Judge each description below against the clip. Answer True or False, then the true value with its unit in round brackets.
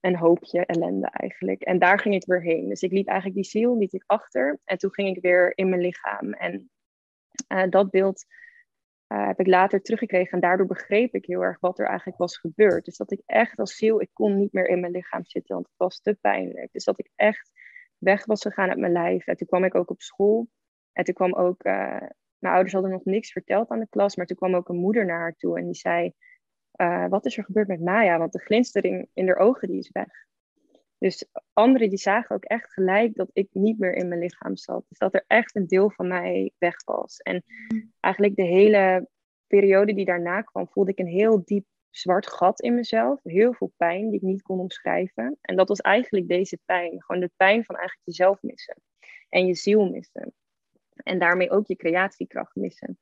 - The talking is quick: True (225 wpm)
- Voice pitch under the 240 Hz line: True (190 Hz)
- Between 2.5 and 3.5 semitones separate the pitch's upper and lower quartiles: True (2.8 semitones)